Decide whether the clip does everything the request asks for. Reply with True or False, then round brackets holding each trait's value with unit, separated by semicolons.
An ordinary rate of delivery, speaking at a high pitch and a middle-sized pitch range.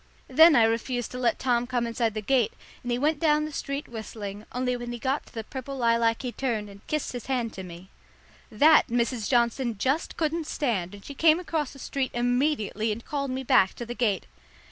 False (215 wpm; 245 Hz; 3.4 semitones)